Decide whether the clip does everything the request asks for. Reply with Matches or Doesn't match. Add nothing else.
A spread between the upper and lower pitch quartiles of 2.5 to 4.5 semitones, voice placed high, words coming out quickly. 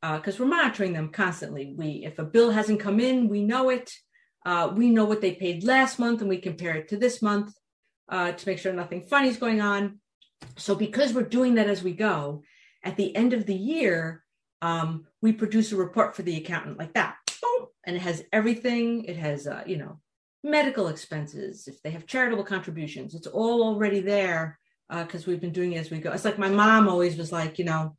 Doesn't match